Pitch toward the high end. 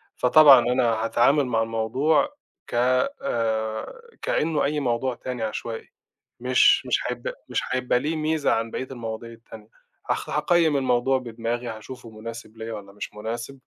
No: low, 120 Hz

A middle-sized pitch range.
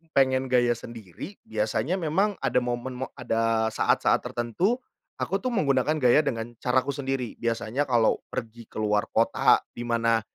Yes: average, 3.2 semitones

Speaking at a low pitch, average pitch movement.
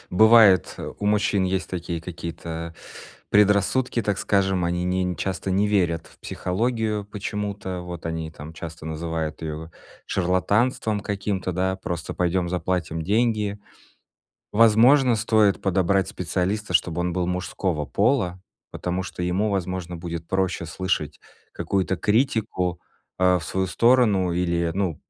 Yes: very low, 95 Hz; average, 3.1 semitones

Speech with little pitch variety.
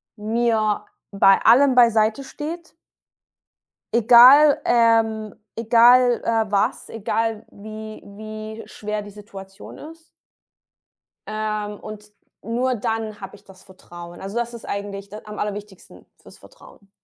Yes: narrow, 2.2 semitones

